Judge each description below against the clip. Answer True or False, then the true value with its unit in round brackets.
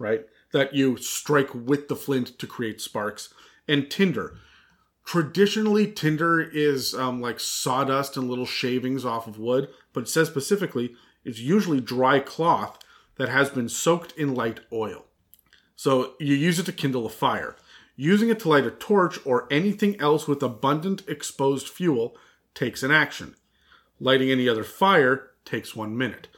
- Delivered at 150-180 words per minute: True (160 wpm)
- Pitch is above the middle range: False (140 Hz)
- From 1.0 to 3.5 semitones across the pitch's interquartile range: False (4.3 semitones)